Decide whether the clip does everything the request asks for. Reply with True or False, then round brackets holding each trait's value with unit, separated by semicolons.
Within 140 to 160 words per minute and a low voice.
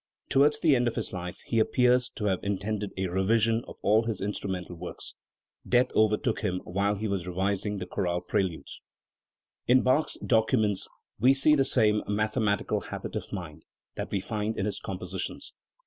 False (170 wpm; 105 Hz)